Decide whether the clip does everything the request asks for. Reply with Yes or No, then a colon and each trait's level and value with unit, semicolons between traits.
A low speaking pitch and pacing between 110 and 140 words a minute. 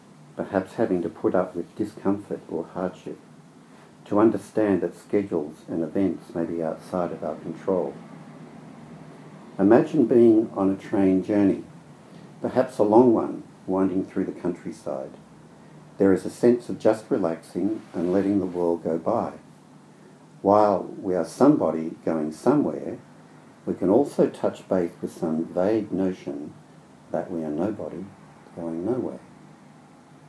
Yes: very low, 90 Hz; slow, 135 wpm